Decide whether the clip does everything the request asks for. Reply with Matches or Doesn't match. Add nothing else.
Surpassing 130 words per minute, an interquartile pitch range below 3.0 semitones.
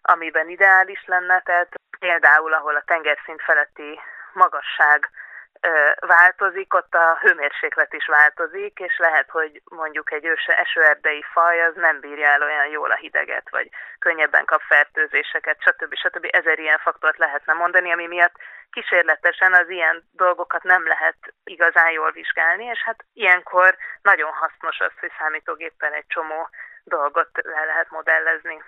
Matches